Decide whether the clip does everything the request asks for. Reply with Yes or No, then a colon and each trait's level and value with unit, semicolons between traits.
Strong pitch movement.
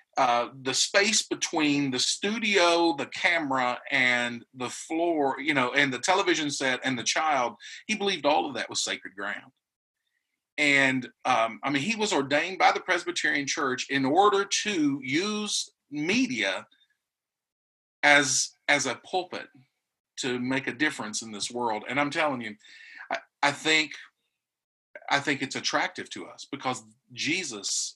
Yes: wide, 7.7 semitones